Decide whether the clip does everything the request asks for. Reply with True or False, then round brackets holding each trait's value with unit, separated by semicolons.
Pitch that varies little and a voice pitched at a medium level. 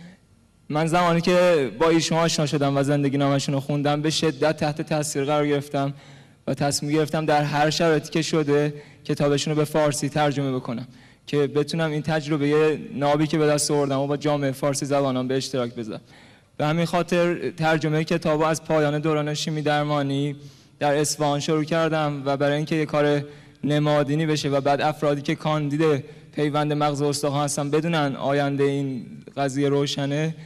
True (1.6 semitones; 150 Hz)